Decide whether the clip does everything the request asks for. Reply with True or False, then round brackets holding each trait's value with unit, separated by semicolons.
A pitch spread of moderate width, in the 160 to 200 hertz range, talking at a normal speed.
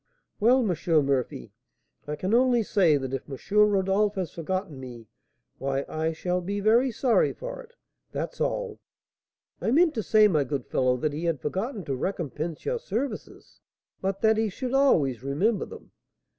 False (7.3 semitones; 190 Hz; 170 wpm)